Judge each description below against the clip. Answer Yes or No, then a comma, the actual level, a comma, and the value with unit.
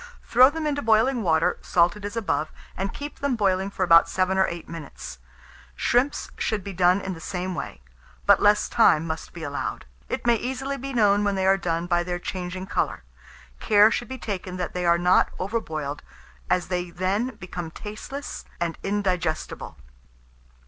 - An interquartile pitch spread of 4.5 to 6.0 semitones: No, average, 4.0 semitones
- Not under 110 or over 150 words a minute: No, average, 180 wpm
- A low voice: No, high, 190 Hz